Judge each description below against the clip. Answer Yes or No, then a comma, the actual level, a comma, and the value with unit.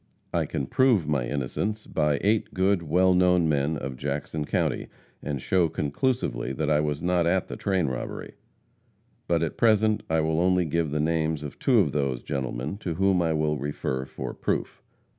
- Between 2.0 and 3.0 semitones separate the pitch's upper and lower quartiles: No, average, 4.1 semitones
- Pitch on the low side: Yes, very low, 80 Hz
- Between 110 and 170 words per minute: No, average, 180 wpm